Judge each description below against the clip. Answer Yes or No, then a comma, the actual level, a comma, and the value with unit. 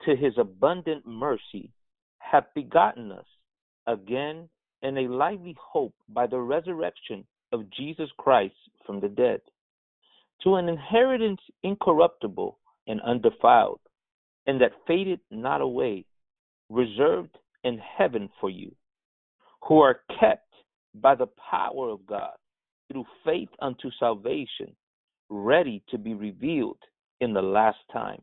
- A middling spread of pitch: No, wide, 8.0 semitones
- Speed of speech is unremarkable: No, slow, 120 wpm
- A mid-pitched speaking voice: Yes, medium, 150 Hz